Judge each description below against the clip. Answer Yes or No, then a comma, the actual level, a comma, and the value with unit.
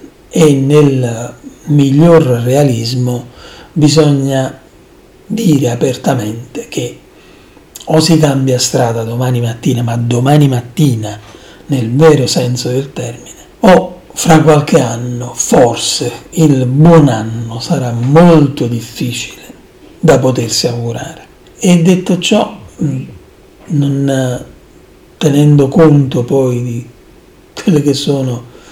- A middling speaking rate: No, slow, 100 wpm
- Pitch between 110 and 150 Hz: Yes, low, 135 Hz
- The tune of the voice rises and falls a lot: No, average, 4.1 semitones